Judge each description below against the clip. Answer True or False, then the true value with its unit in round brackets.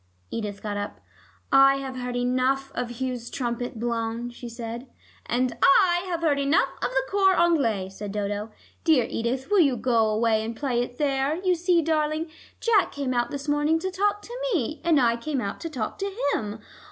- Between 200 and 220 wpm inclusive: False (190 wpm)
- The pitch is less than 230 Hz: False (260 Hz)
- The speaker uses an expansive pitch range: True (5.7 semitones)